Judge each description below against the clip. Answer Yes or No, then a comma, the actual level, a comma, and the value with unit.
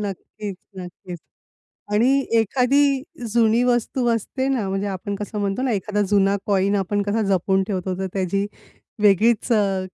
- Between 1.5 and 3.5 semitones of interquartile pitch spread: Yes, average, 2.9 semitones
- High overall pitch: Yes, high, 205 Hz